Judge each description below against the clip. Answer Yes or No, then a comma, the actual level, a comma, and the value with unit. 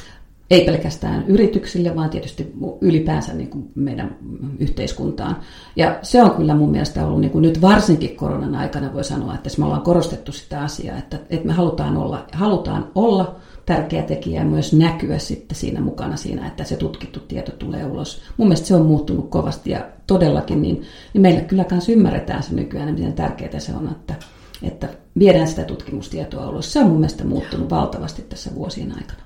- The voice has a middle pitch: Yes, medium, 165 Hz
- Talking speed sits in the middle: No, fast, 170 wpm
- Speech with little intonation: No, average, 4.9 semitones